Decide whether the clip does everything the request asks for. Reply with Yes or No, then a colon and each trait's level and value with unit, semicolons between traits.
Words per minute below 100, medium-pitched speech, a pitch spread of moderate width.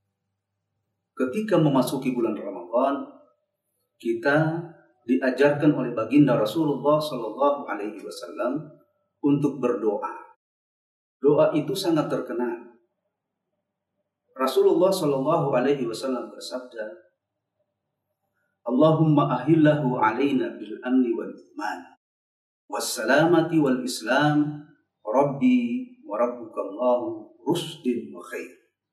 Yes: slow, 85 wpm; medium, 145 Hz; average, 4.6 semitones